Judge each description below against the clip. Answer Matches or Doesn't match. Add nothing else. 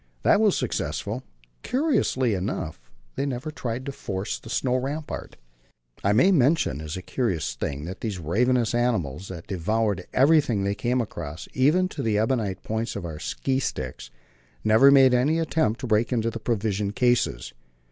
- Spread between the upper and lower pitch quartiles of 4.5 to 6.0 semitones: Matches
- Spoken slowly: Doesn't match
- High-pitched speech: Doesn't match